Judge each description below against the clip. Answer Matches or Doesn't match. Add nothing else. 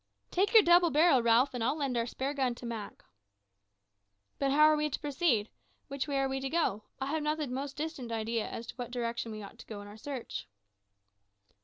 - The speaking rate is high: Matches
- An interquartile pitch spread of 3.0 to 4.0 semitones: Doesn't match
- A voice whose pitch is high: Matches